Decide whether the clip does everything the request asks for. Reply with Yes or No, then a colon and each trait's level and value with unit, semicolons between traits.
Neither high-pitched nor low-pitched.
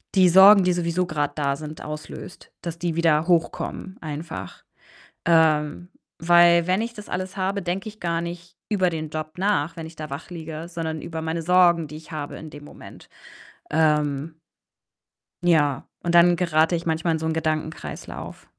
Yes: medium, 165 Hz